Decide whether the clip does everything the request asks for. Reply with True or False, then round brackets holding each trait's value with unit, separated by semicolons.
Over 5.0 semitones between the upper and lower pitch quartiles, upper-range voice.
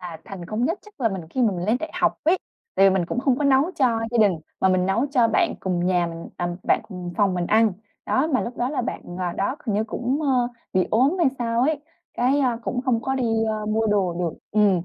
True (5.4 semitones; 225 Hz)